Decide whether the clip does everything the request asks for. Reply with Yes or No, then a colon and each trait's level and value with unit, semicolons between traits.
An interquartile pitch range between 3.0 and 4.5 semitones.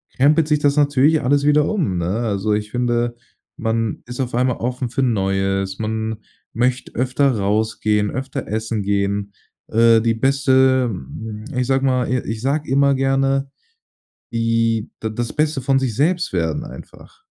Yes: average, 3.7 semitones